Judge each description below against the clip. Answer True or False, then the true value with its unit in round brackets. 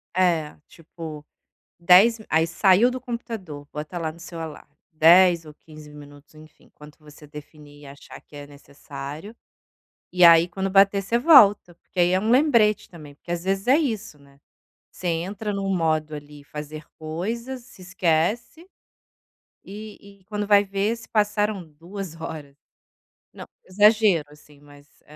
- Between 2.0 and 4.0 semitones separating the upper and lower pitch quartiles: False (5.3 semitones)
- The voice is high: False (175 Hz)